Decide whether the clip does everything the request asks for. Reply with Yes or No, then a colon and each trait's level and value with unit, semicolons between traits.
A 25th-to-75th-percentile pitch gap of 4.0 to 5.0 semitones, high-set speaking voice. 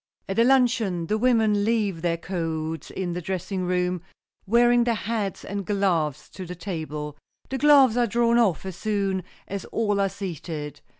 Yes: average, 4.6 semitones; high, 195 Hz